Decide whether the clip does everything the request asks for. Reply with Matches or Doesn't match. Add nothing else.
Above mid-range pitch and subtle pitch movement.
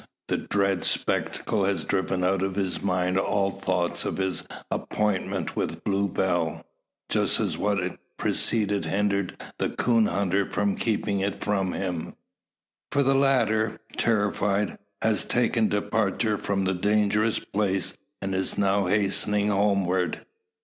Doesn't match